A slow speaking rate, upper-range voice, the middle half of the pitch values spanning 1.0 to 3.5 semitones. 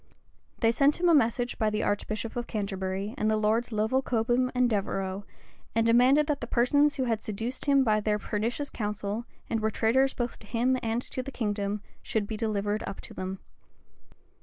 No: average, 190 wpm; high, 225 Hz; average, 3.0 semitones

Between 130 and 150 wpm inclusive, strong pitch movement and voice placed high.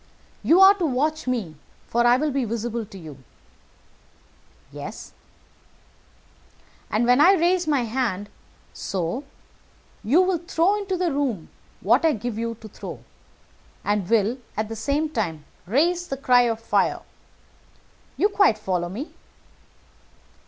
Yes: average, 140 wpm; wide, 6.6 semitones; high, 245 Hz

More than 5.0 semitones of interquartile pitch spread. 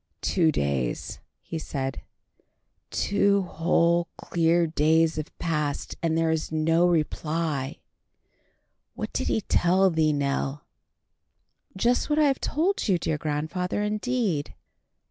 No: average, 3.5 semitones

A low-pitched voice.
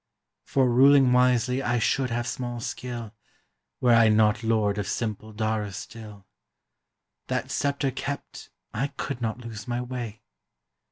Yes: low, 120 Hz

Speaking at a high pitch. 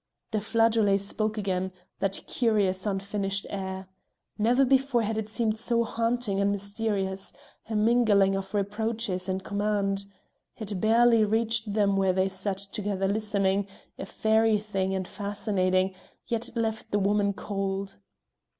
Yes: high, 205 Hz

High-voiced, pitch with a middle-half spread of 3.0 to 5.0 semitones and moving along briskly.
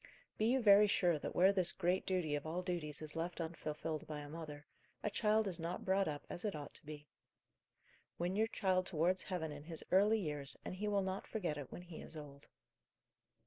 No: medium, 175 Hz; average, 4.0 semitones; fast, 215 wpm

